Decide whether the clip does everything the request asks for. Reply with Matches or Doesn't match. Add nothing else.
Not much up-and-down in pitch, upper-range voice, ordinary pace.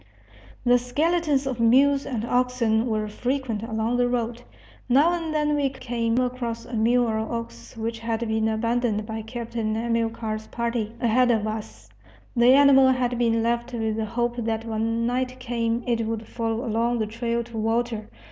Matches